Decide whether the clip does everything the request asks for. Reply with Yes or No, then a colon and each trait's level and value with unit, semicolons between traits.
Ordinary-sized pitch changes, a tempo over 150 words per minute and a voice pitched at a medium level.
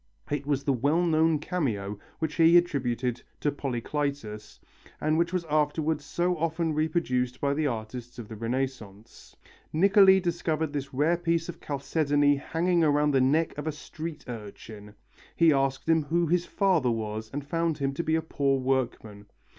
Yes: average, 4.3 semitones; average, 165 wpm; medium, 145 Hz